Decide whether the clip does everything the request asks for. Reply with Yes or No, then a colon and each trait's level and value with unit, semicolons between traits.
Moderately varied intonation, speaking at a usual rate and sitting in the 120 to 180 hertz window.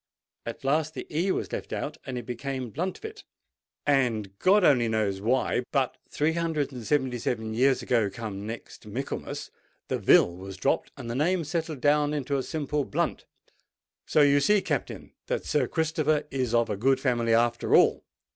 Yes: average, 4.3 semitones; average, 175 wpm; low, 135 Hz